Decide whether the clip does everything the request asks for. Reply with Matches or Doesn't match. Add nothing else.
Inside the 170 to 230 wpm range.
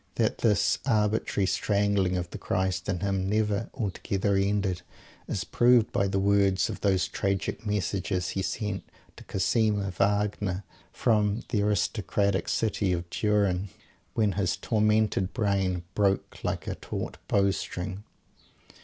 Doesn't match